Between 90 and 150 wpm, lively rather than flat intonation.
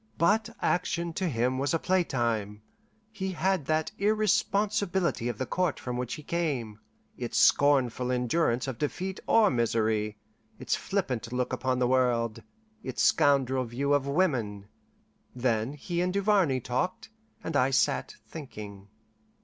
Yes: average, 140 wpm; wide, 6.4 semitones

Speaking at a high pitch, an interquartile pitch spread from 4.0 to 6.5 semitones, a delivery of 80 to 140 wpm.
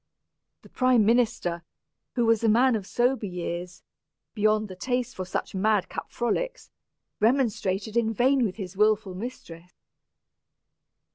Yes: high, 215 Hz; average, 4.3 semitones; slow, 135 wpm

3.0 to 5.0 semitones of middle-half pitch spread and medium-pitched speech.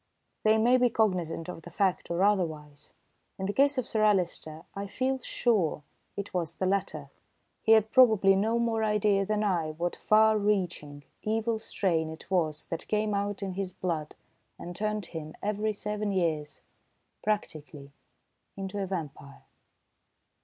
No: average, 4.4 semitones; high, 195 Hz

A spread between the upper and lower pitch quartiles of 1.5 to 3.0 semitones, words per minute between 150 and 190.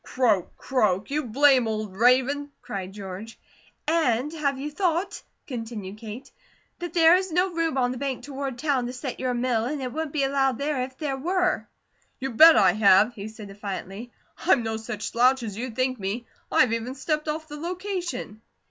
No: average, 5.1 semitones; average, 185 wpm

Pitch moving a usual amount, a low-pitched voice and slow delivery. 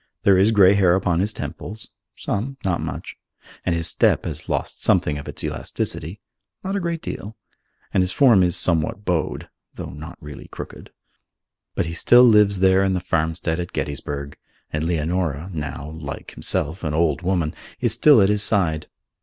No: average, 4.2 semitones; very low, 90 Hz; average, 175 wpm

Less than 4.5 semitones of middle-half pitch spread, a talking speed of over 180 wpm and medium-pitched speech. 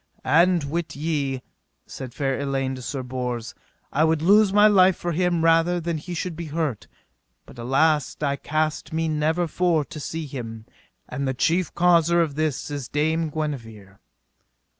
No: average, 3.8 semitones; average, 170 wpm; medium, 155 Hz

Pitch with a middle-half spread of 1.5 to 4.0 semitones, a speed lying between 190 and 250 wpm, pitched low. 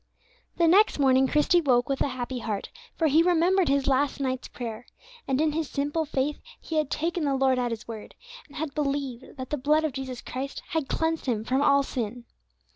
No: average, 3.2 semitones; fast, 205 wpm; very high, 275 Hz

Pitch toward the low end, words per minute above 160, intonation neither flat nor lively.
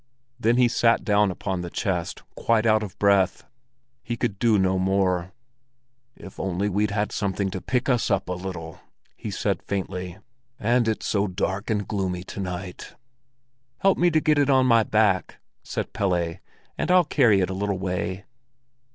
Yes: low, 100 Hz; average, 175 wpm; average, 3.4 semitones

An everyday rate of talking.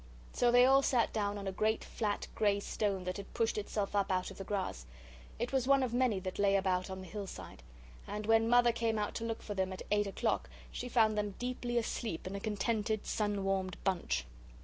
No: fast, 220 wpm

